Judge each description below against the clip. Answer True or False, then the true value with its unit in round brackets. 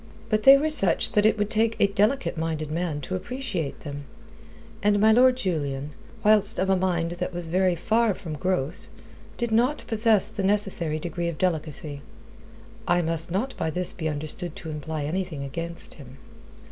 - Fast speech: False (175 wpm)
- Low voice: False (180 Hz)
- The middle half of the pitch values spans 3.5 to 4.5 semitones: False (5.1 semitones)